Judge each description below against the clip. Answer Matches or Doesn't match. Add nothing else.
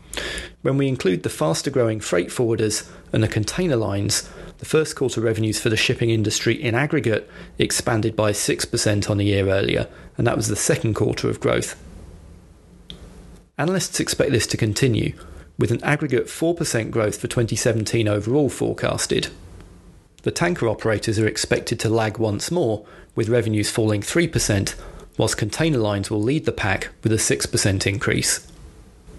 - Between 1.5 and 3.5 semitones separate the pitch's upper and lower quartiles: Matches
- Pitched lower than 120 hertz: Matches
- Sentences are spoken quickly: Doesn't match